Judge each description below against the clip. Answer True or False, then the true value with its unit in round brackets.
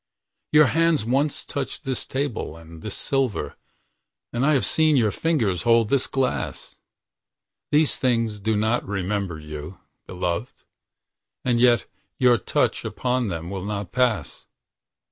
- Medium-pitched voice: False (115 Hz)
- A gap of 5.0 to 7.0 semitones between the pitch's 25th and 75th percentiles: True (5.3 semitones)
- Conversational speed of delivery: False (125 wpm)